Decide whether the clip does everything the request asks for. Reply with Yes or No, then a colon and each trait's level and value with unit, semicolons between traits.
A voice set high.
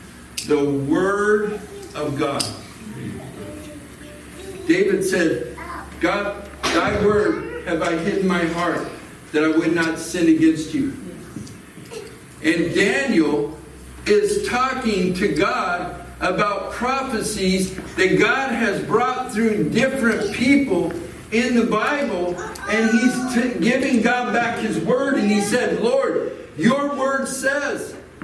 Yes: high, 210 Hz